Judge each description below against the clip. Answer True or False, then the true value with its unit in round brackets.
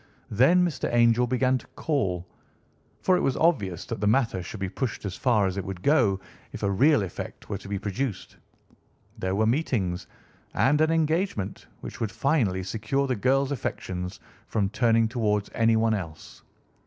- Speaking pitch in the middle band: False (110 Hz)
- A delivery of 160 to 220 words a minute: True (170 wpm)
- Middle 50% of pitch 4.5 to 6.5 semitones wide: True (5.5 semitones)